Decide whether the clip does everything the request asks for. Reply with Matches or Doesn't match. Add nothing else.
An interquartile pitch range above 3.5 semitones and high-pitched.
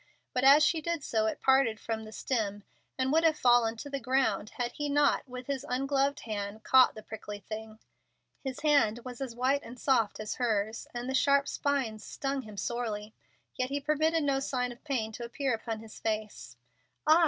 Matches